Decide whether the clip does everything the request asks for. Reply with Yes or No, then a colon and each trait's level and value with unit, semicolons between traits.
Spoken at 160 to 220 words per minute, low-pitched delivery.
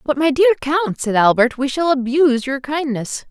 No: average, 200 wpm; very high, 275 Hz